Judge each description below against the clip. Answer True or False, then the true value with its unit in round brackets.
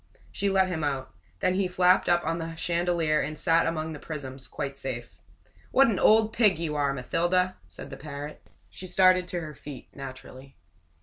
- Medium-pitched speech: True (165 Hz)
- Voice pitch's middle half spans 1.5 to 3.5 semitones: False (4.4 semitones)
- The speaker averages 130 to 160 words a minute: False (185 wpm)